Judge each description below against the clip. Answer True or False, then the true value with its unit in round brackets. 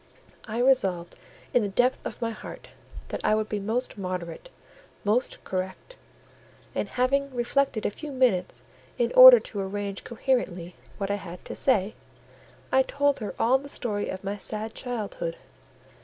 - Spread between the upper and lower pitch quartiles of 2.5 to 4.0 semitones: False (4.9 semitones)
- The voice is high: True (220 Hz)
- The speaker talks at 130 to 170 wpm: True (155 wpm)